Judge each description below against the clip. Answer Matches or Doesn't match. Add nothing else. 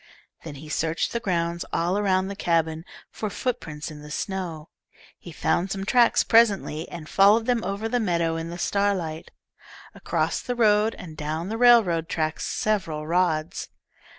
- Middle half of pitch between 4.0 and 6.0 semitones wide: Matches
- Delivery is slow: Doesn't match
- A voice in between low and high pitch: Matches